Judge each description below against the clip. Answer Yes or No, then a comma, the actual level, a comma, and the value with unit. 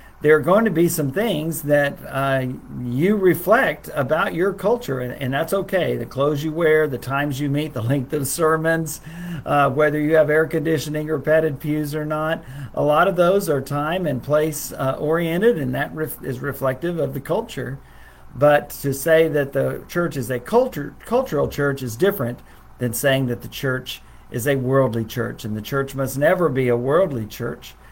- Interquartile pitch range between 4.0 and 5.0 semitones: No, average, 3.3 semitones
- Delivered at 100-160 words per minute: No, average, 195 wpm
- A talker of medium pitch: Yes, medium, 145 Hz